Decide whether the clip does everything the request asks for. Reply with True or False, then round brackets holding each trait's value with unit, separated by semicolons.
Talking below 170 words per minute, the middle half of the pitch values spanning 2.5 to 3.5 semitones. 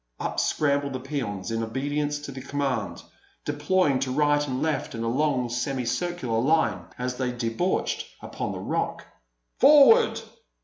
True (145 wpm; 3.2 semitones)